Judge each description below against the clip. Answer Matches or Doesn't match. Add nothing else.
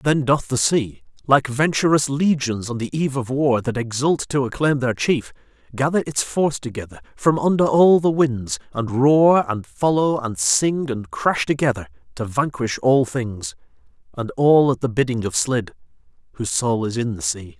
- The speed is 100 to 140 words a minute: Doesn't match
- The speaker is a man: Matches